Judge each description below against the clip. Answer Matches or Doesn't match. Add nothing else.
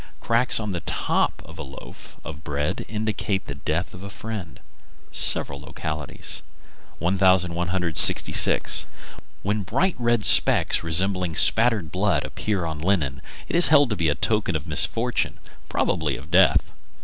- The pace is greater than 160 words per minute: Doesn't match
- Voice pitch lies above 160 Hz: Doesn't match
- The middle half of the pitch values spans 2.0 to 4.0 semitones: Doesn't match